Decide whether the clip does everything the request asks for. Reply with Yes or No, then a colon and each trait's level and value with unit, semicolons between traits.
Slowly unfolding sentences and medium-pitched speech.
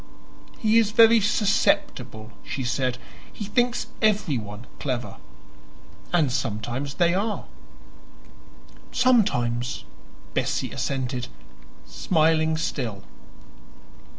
Yes: slow, 80 wpm; medium, 155 Hz